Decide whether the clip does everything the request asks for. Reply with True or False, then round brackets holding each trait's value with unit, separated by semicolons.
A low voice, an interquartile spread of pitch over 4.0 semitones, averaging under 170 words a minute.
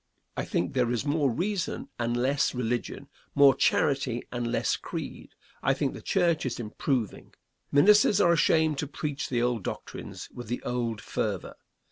False (130 Hz; 3.7 semitones; 160 wpm)